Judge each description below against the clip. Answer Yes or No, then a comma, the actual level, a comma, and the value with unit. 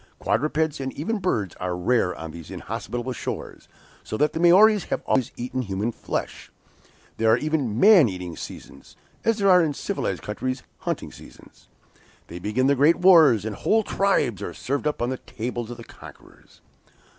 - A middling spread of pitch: No, wide, 6.6 semitones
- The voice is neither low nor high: No, low, 130 Hz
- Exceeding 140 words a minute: Yes, average, 175 wpm